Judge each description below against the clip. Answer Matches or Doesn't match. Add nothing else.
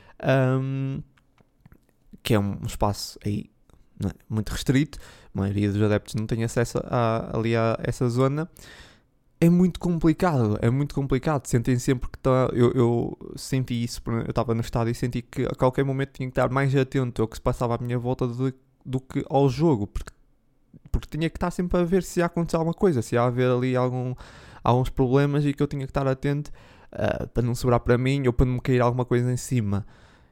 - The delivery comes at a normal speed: Doesn't match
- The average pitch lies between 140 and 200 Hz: Doesn't match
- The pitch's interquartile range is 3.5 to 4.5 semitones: Doesn't match